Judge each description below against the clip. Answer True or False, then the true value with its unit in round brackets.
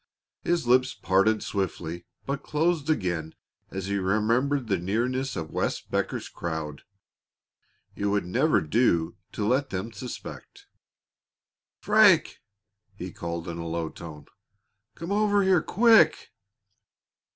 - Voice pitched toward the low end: True (110 Hz)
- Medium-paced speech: False (120 wpm)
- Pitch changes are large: True (8.8 semitones)